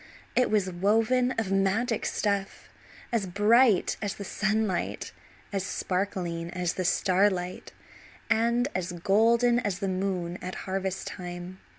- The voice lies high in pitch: Yes, high, 195 Hz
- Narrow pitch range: No, average, 3.2 semitones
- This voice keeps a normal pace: No, slow, 125 wpm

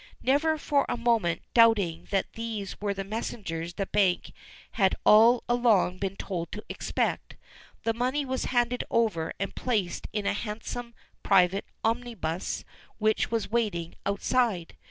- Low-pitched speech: No, high, 215 Hz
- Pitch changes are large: No, average, 3.7 semitones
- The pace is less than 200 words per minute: Yes, average, 140 wpm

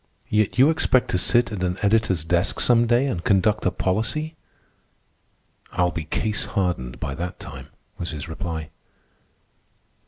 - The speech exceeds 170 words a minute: No, average, 150 wpm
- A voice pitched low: Yes, very low, 95 Hz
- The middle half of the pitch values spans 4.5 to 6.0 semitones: Yes, average, 4.8 semitones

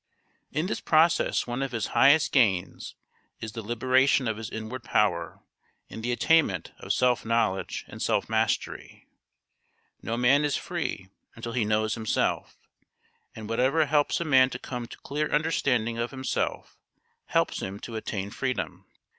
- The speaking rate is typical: Yes, average, 155 wpm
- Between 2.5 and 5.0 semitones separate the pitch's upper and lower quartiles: Yes, average, 3.8 semitones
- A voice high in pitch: No, low, 120 Hz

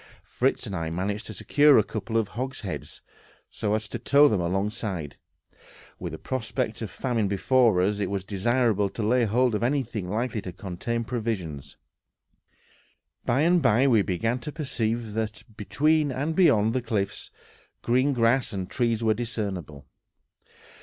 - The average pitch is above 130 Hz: No, low, 110 Hz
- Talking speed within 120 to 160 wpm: Yes, average, 155 wpm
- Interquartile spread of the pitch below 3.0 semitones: No, average, 3.9 semitones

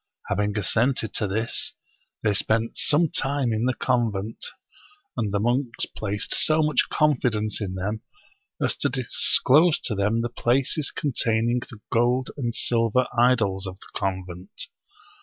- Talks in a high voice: No, low, 115 Hz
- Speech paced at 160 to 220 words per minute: No, average, 145 wpm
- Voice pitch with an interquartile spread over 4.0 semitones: No, average, 3.6 semitones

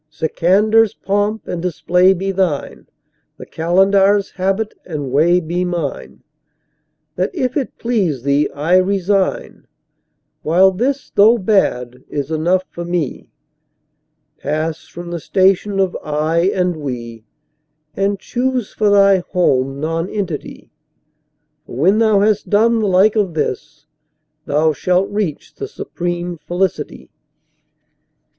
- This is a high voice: No, medium, 180 Hz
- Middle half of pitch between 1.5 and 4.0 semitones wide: No, average, 4.4 semitones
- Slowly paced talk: Yes, slow, 115 wpm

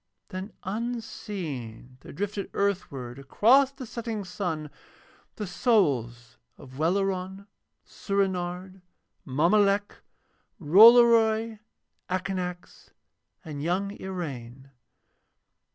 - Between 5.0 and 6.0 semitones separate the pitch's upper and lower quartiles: Yes, wide, 5.6 semitones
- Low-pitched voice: No, high, 190 Hz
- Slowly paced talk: Yes, slow, 75 wpm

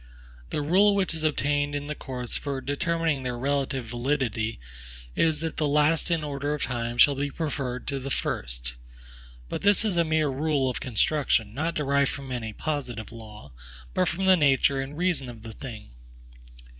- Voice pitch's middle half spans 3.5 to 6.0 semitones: Yes, average, 3.9 semitones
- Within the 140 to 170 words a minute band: No, average, 180 wpm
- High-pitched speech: No, medium, 140 Hz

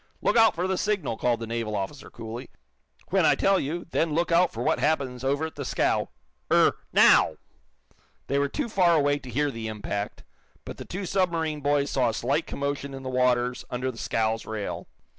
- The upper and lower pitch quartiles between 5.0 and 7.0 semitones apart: Yes, wide, 5.4 semitones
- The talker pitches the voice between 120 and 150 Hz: Yes, medium, 140 Hz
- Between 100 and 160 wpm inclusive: No, average, 200 wpm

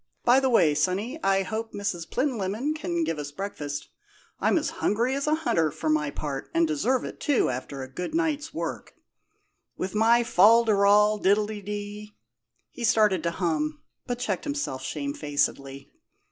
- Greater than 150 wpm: Yes, average, 165 wpm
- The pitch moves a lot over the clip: Yes, wide, 7.6 semitones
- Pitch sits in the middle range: No, high, 205 Hz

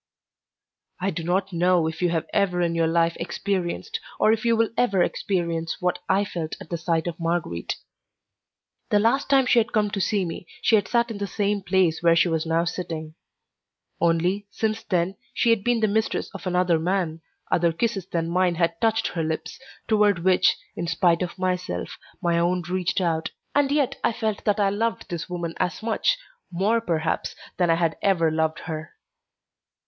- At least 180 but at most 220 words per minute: Yes, average, 190 wpm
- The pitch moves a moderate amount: Yes, average, 3.6 semitones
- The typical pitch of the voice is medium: Yes, medium, 180 Hz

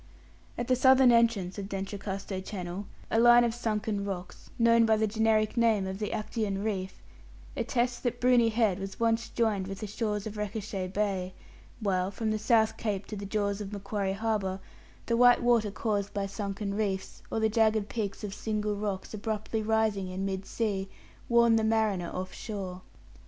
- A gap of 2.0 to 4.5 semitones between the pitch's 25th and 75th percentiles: Yes, narrow, 2.4 semitones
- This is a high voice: Yes, high, 210 Hz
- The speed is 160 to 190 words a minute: Yes, average, 180 wpm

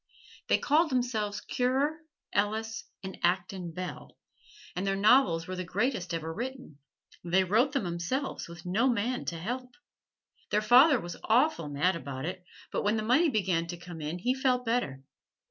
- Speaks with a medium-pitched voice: No, high, 205 Hz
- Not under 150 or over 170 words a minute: Yes, average, 165 wpm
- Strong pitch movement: Yes, wide, 6.3 semitones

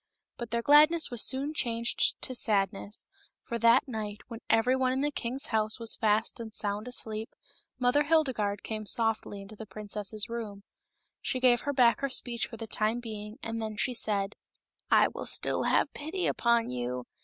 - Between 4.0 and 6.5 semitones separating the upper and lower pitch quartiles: No, average, 3.0 semitones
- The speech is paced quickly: No, average, 190 wpm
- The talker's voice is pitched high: Yes, high, 230 Hz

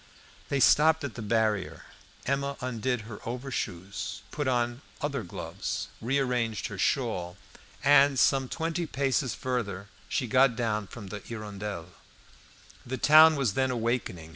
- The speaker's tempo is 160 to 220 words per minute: No, slow, 135 wpm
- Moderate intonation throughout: Yes, average, 4.7 semitones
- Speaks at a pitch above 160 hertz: No, low, 120 Hz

